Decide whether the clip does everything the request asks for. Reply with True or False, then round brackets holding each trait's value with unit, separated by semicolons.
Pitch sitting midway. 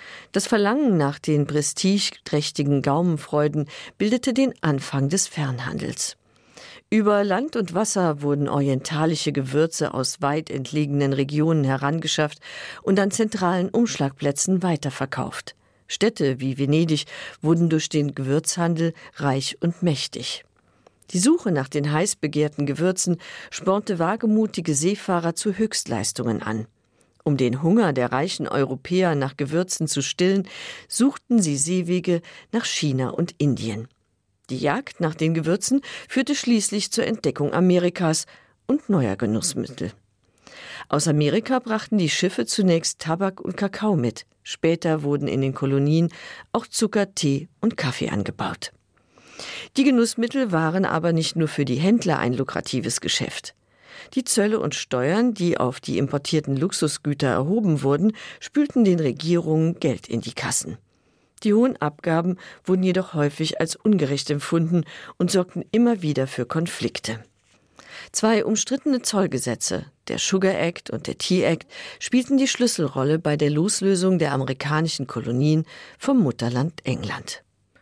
True (160 Hz)